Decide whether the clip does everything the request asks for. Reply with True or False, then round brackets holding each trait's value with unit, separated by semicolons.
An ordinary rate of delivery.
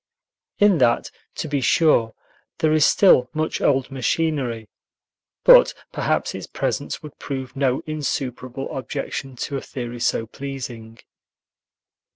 False (125 wpm)